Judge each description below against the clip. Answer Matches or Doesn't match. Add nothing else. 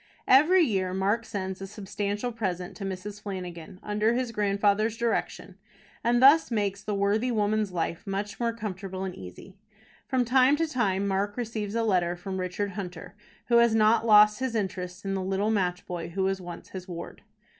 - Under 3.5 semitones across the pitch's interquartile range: Matches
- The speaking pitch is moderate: Doesn't match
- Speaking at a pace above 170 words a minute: Matches